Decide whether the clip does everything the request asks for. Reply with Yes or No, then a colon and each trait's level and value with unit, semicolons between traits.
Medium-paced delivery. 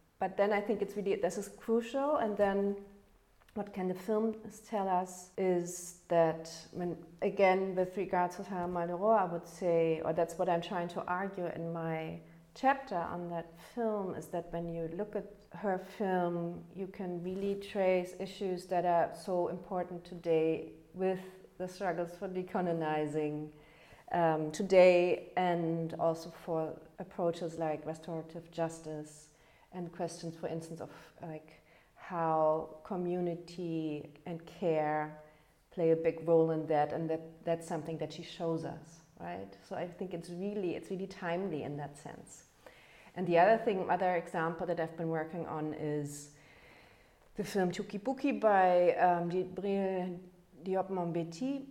Yes: average, 150 wpm